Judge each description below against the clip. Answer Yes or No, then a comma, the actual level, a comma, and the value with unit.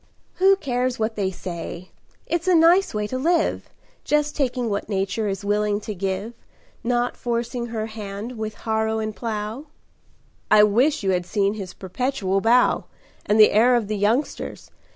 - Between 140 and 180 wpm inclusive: Yes, average, 165 wpm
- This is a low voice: No, high, 220 Hz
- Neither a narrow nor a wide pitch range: Yes, average, 3.6 semitones